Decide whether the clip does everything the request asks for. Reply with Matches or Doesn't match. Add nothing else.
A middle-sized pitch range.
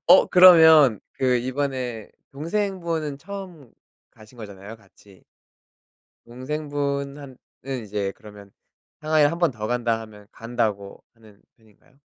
Doesn't match